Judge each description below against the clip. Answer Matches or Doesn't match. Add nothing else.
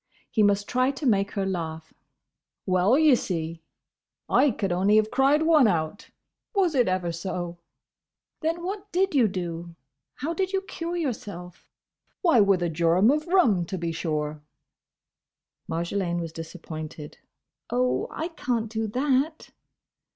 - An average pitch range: Doesn't match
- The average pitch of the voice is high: Matches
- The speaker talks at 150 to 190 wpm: Doesn't match